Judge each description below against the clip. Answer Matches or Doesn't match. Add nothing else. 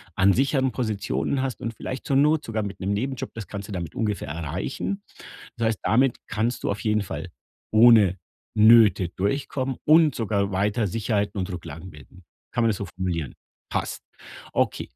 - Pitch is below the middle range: Matches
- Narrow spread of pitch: Doesn't match